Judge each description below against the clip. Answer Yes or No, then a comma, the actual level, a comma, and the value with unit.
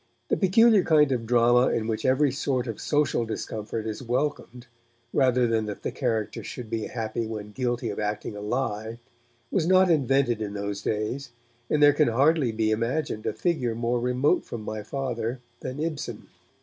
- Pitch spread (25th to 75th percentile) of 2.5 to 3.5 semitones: No, average, 4.0 semitones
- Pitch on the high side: No, low, 120 Hz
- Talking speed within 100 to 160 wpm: No, average, 175 wpm